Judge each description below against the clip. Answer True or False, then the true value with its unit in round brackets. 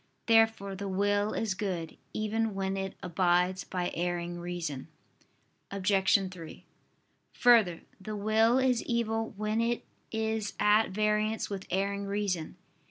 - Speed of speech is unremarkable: False (125 wpm)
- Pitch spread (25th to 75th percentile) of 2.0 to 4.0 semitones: True (2.9 semitones)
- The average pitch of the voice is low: False (200 Hz)